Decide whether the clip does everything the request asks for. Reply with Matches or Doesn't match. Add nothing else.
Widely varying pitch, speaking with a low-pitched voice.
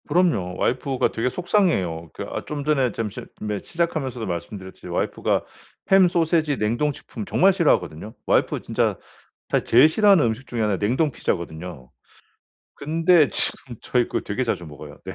Matches